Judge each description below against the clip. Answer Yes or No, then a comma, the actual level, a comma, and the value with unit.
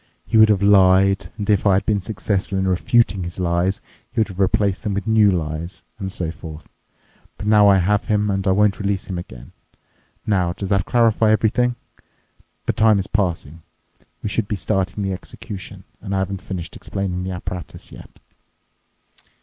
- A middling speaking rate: Yes, average, 180 wpm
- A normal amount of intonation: No, narrow, 2.2 semitones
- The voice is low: Yes, very low, 95 Hz